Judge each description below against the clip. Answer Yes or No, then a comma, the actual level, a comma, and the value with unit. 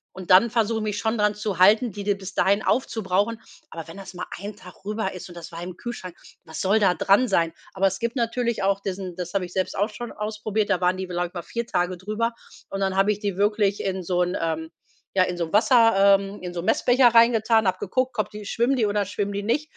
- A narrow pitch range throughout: No, average, 3.1 semitones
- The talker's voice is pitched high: Yes, high, 200 Hz